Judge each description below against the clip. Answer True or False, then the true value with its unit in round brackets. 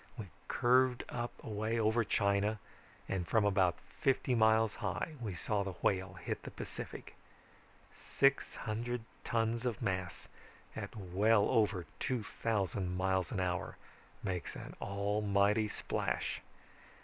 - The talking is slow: True (125 wpm)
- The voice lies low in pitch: True (105 Hz)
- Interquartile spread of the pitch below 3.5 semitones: True (3.0 semitones)